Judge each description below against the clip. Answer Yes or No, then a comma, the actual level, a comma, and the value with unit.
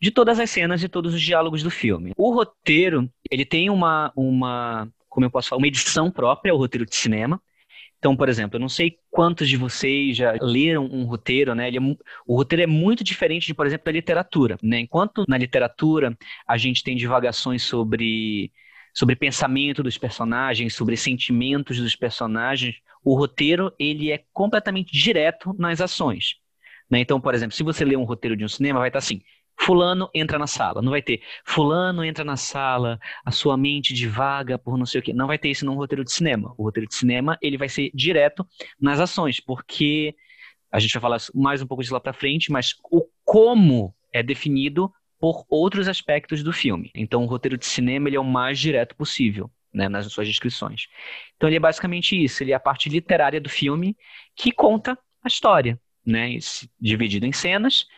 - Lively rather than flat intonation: No, average, 4.7 semitones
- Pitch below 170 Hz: Yes, medium, 140 Hz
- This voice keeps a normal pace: No, fast, 195 wpm